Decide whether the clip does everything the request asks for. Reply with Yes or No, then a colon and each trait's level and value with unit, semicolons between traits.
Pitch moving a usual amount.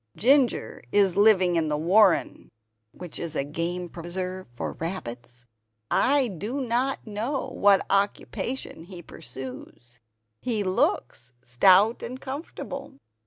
No: wide, 5.8 semitones